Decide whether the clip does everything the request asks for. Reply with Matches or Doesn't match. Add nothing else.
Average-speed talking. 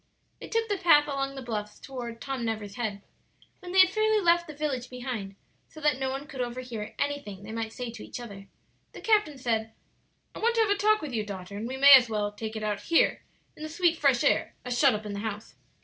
Doesn't match